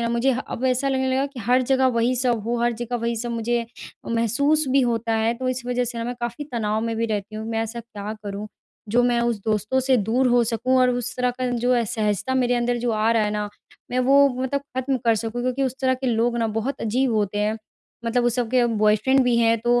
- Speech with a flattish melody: Yes, narrow, 2.1 semitones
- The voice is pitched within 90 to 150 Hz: No, high, 240 Hz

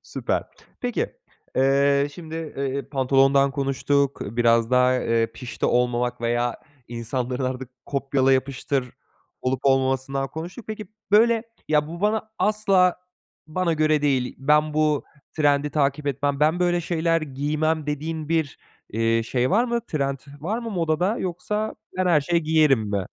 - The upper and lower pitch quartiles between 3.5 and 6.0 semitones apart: Yes, average, 4.0 semitones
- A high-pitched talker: No, medium, 145 Hz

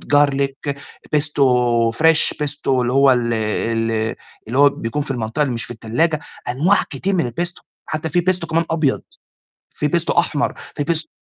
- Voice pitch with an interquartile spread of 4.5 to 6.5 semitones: Yes, average, 4.8 semitones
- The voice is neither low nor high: Yes, medium, 145 Hz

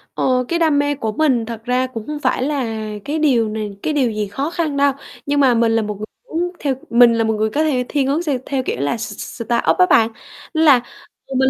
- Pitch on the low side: No, very high, 255 Hz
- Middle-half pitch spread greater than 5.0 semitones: No, average, 4.3 semitones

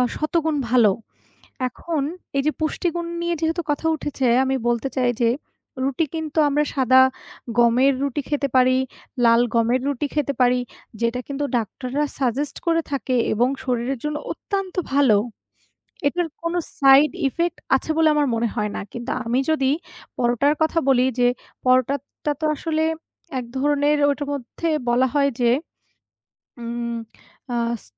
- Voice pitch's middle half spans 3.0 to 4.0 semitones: Yes, average, 3.6 semitones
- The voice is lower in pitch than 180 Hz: No, very high, 275 Hz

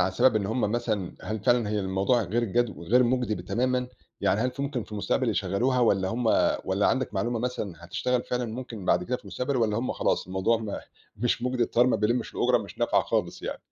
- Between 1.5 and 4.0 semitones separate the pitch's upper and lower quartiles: Yes, average, 3.3 semitones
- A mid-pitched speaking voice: No, low, 115 Hz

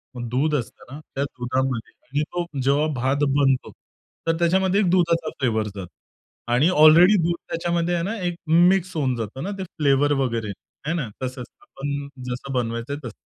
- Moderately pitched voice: Yes, medium, 145 Hz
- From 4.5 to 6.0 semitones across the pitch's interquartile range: Yes, average, 5.0 semitones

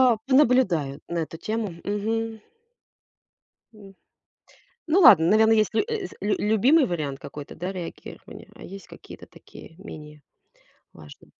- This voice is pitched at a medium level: No, high, 205 Hz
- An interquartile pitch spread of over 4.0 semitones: Yes, wide, 5.5 semitones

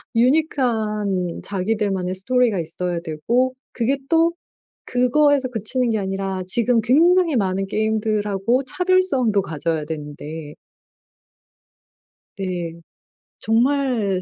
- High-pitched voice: Yes, high, 215 Hz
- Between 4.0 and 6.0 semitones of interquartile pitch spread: Yes, wide, 5.4 semitones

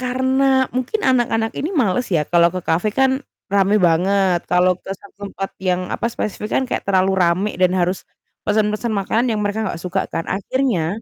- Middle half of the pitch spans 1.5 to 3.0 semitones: No, average, 4.8 semitones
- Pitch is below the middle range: No, high, 200 Hz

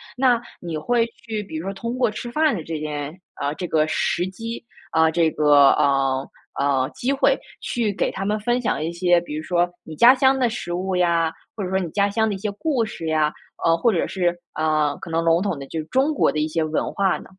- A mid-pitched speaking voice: Yes, medium, 175 Hz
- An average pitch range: No, wide, 5.9 semitones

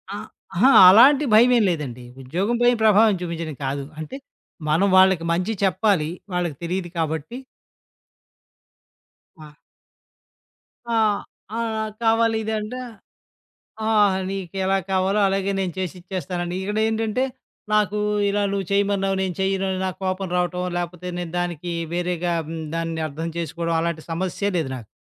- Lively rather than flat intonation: No, average, 3.4 semitones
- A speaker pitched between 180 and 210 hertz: Yes, medium, 185 Hz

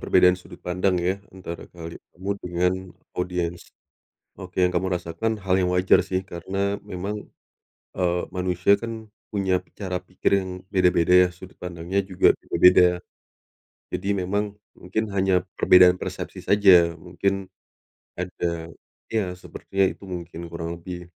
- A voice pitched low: Yes, very low, 90 Hz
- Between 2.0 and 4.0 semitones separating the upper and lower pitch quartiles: No, narrow, 1.4 semitones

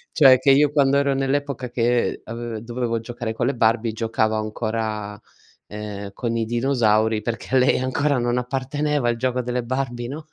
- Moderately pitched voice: No, low, 120 Hz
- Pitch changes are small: No, average, 3.0 semitones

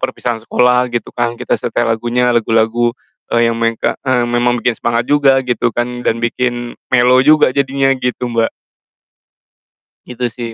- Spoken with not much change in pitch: Yes, narrow, 1.1 semitones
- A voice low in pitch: Yes, low, 120 Hz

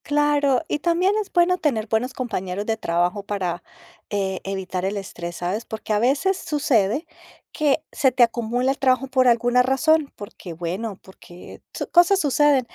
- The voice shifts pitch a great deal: Yes, wide, 6.6 semitones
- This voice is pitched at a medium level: No, high, 240 Hz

